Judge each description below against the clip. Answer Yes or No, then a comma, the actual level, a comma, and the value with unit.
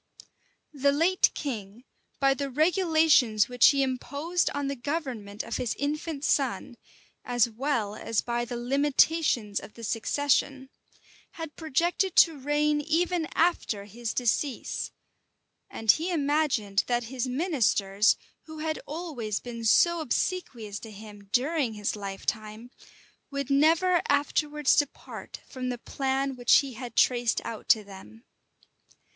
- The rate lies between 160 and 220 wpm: No, slow, 135 wpm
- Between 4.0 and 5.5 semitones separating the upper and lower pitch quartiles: Yes, average, 4.9 semitones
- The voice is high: Yes, very high, 265 Hz